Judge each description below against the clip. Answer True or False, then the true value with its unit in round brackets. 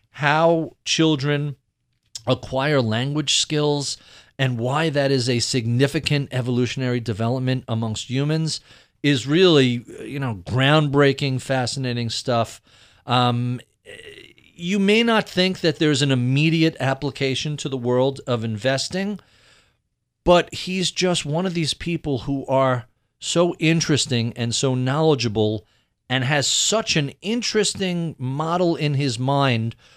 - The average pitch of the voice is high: False (135 Hz)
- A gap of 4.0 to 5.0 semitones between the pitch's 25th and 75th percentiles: True (4.3 semitones)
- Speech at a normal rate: False (120 wpm)